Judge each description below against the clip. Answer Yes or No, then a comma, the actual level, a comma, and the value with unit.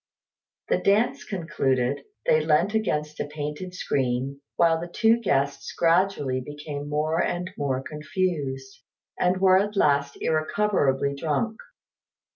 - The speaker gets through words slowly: Yes, slow, 120 wpm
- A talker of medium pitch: Yes, medium, 150 Hz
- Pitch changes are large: No, average, 4.8 semitones